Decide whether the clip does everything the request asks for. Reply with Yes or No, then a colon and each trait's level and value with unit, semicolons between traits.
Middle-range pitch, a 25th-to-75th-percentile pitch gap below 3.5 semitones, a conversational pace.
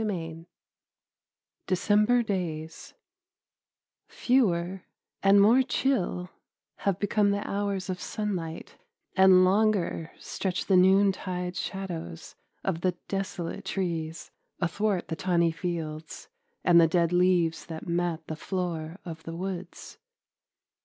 No: medium, 180 Hz; average, 2.9 semitones; slow, 110 wpm